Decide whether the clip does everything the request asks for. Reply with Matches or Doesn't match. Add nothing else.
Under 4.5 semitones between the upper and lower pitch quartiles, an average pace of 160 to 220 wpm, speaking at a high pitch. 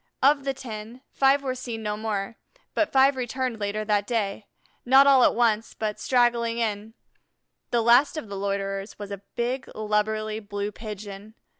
Matches